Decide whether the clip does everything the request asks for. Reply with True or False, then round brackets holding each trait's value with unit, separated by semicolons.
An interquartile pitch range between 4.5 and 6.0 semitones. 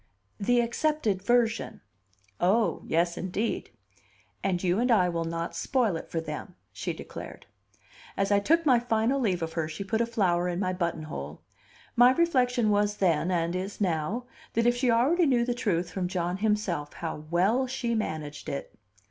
True (5.6 semitones)